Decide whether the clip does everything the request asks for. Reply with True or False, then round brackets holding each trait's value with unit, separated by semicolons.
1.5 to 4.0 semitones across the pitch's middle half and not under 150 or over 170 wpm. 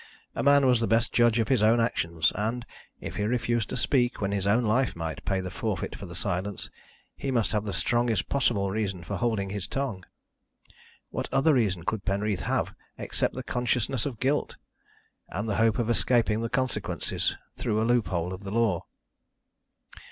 False (3.6 semitones; 185 wpm)